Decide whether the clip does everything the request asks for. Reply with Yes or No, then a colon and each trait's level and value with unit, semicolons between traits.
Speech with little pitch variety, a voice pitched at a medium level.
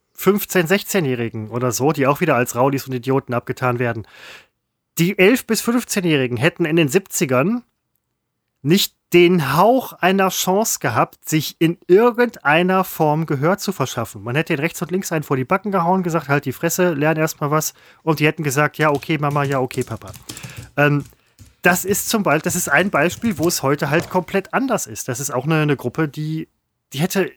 No: wide, 5.4 semitones; medium, 160 Hz